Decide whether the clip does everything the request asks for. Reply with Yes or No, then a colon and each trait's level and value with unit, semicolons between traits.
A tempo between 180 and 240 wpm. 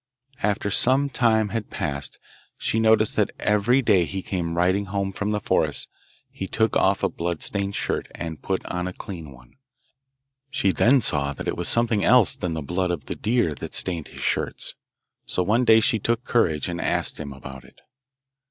Yes: average, 190 wpm